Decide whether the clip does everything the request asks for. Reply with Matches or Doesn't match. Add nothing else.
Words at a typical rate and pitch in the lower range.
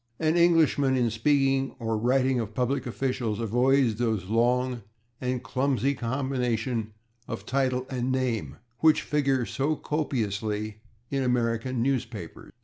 Doesn't match